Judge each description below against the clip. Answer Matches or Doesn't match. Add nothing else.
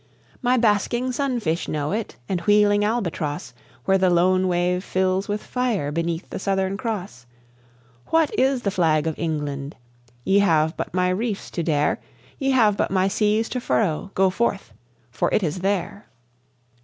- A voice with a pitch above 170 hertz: Matches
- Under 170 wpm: Matches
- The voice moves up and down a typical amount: Matches